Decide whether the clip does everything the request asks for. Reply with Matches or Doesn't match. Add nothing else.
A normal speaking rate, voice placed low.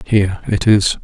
Matches